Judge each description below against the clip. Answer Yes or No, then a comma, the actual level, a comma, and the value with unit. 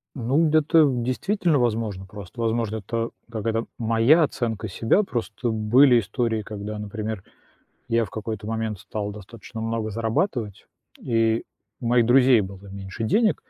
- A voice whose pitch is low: Yes, low, 115 Hz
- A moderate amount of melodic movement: No, narrow, 2.3 semitones